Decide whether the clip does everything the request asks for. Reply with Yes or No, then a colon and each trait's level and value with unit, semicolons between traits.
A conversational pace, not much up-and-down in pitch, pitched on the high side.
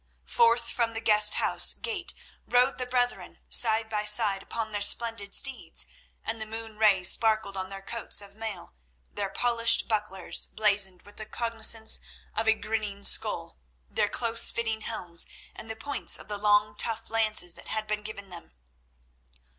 Yes: average, 165 wpm; narrow, 1.9 semitones; high, 220 Hz